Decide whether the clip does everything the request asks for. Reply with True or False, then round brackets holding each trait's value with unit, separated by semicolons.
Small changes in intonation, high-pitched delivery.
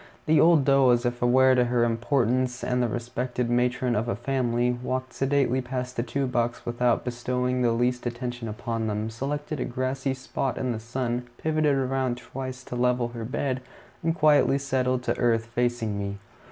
False (1.6 semitones; 125 Hz)